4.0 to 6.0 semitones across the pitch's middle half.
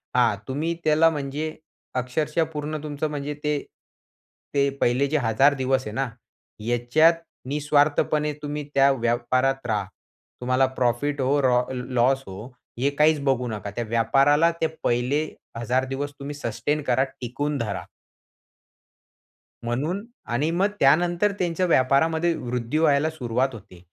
No: average, 3.6 semitones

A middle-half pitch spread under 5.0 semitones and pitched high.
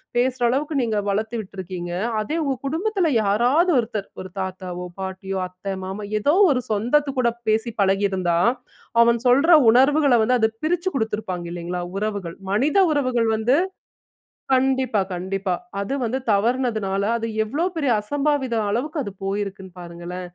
No: wide, 5.4 semitones; high, 220 Hz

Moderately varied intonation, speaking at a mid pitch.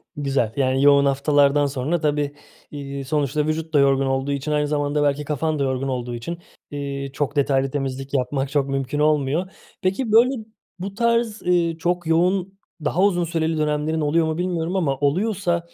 Yes: average, 3.6 semitones; medium, 150 Hz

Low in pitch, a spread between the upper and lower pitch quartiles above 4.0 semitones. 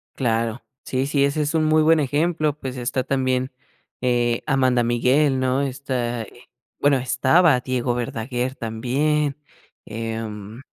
No: low, 130 Hz; average, 2.8 semitones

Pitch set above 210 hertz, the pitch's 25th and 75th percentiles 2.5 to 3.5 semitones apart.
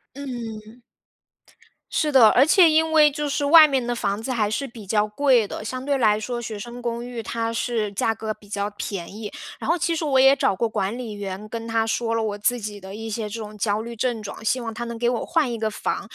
Yes: high, 230 Hz; average, 3.2 semitones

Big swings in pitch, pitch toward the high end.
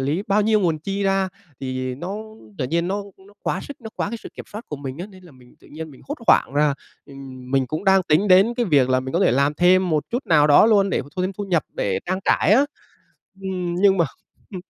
No: wide, 5.7 semitones; medium, 175 Hz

